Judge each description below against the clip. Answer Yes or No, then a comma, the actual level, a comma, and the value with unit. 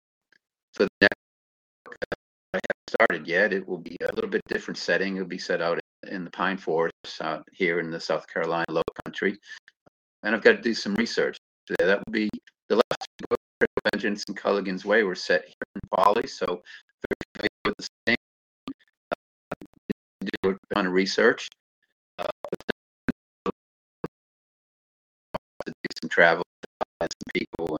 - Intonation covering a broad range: Yes, wide, 5.8 semitones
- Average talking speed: Yes, average, 160 wpm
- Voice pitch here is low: Yes, very low, 90 Hz